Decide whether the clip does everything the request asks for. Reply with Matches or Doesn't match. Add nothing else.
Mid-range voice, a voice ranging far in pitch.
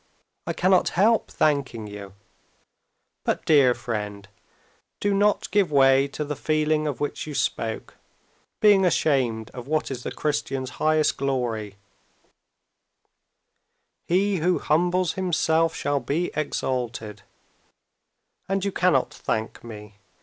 Matches